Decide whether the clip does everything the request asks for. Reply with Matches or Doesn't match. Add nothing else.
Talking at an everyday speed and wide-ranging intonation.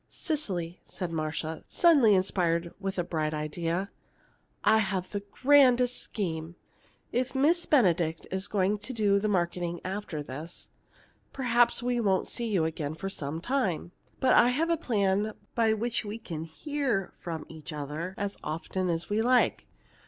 Matches